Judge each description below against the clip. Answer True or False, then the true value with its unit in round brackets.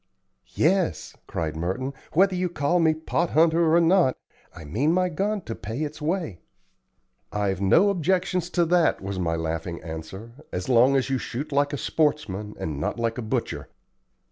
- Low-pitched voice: False (145 Hz)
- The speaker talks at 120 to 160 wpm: False (170 wpm)